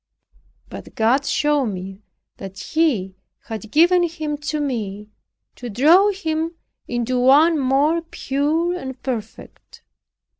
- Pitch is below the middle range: No, very high, 275 Hz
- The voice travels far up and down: Yes, wide, 6.0 semitones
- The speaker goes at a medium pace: No, slow, 115 wpm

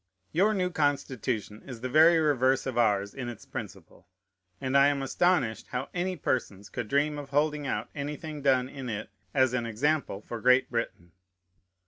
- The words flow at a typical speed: Yes, average, 170 wpm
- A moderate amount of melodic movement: Yes, average, 3.9 semitones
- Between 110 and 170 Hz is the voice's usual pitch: Yes, low, 135 Hz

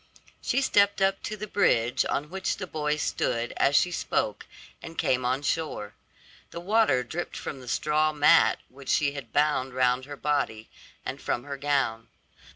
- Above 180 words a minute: No, average, 170 wpm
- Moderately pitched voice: Yes, medium, 145 Hz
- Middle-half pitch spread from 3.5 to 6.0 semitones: Yes, average, 4.7 semitones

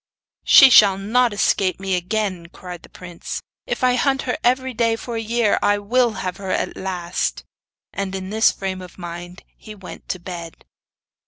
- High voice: Yes, high, 195 Hz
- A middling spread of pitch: Yes, average, 4.0 semitones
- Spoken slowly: No, average, 180 wpm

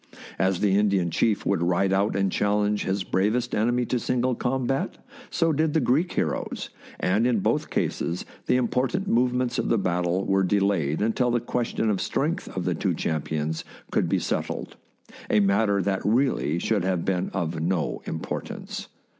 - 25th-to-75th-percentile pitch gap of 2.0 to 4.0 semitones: No, average, 4.7 semitones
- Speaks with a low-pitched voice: Yes, low, 100 Hz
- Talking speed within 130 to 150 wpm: No, average, 170 wpm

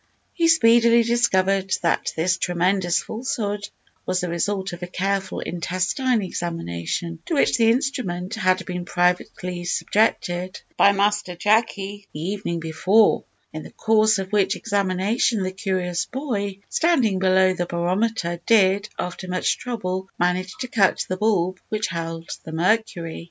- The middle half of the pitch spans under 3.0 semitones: No, average, 3.4 semitones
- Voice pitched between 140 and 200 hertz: Yes, high, 190 Hz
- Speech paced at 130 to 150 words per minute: Yes, average, 140 wpm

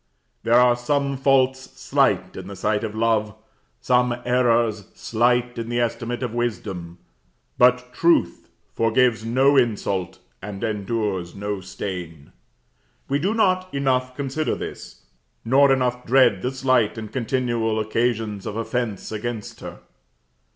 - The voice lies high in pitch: No, low, 120 Hz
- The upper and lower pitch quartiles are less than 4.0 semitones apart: Yes, average, 3.2 semitones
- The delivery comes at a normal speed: No, slow, 130 wpm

